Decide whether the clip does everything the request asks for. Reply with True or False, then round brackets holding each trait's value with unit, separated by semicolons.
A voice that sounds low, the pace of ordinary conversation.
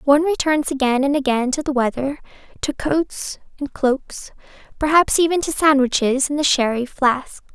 False (280 Hz; 160 wpm)